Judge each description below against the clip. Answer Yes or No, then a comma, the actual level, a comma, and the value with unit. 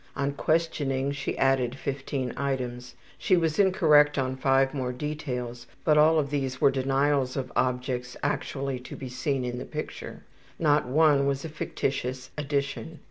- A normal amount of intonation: No, narrow, 2.3 semitones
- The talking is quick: No, average, 155 wpm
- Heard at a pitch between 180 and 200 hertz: No, low, 135 Hz